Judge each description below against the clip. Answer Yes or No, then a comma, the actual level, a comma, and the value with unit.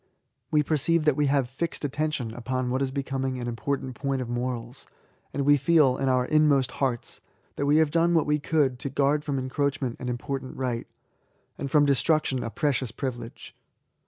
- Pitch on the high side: No, low, 135 Hz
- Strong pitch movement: No, narrow, 2.5 semitones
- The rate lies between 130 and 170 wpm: No, average, 190 wpm